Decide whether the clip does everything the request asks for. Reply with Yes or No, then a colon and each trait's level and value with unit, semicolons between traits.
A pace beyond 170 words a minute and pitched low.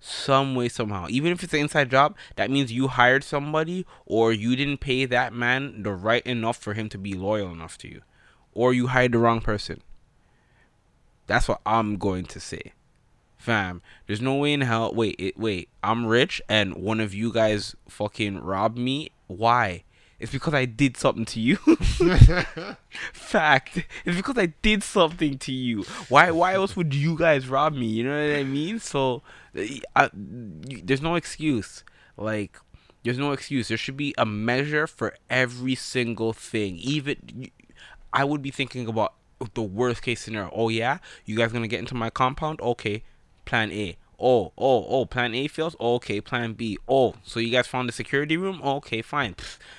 Yes: average, 180 wpm; low, 120 Hz